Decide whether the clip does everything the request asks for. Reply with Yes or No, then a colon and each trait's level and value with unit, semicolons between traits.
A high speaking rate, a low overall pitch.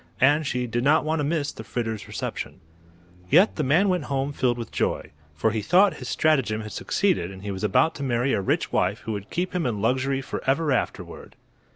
Yes: fast, 215 wpm; low, 130 Hz